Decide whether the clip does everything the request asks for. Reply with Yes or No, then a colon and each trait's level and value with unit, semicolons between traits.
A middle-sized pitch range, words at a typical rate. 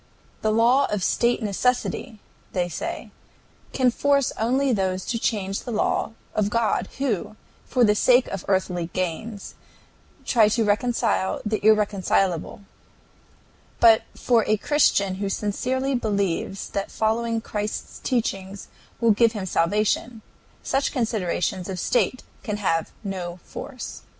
No: average, 3.6 semitones; slow, 130 wpm